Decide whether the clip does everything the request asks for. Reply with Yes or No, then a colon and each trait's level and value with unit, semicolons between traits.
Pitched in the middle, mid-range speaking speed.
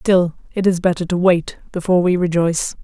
Yes: medium, 175 Hz; average, 190 wpm